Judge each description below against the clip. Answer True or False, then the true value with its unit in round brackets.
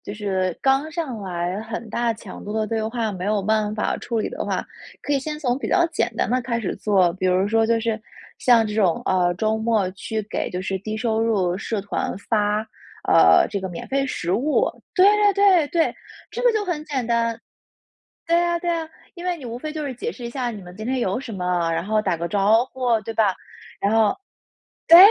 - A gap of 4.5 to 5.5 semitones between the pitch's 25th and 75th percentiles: True (5.0 semitones)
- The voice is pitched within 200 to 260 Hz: True (225 Hz)